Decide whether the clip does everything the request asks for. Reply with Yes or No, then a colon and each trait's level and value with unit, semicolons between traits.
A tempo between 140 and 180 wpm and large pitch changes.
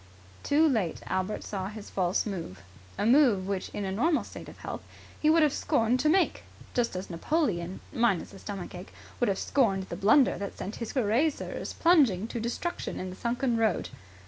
No: average, 190 wpm; wide, 5.9 semitones